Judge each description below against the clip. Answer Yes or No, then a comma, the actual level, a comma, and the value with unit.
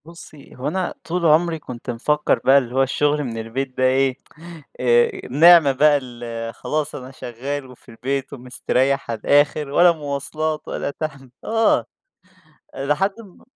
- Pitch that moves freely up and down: No, average, 3.2 semitones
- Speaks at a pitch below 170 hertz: Yes, medium, 140 Hz